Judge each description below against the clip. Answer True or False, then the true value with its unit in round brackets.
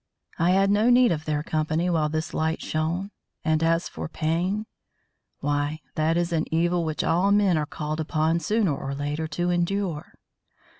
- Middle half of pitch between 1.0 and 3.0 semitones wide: True (2.4 semitones)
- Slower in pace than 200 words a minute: True (170 wpm)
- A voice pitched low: False (165 Hz)